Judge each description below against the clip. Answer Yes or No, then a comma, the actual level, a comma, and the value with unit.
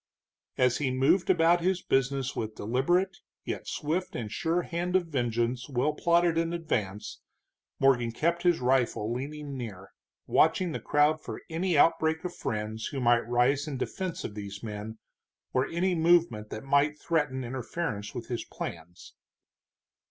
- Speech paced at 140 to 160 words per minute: Yes, average, 150 wpm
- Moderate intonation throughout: No, wide, 6.0 semitones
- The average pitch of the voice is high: No, low, 135 Hz